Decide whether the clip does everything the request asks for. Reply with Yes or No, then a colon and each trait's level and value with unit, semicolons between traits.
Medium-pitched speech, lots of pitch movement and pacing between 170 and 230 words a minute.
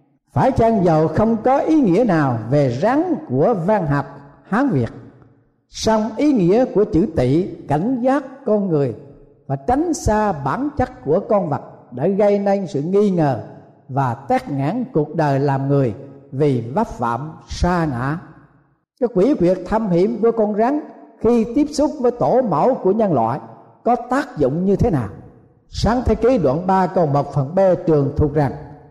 Yes: medium, 165 Hz; wide, 8.3 semitones; average, 180 wpm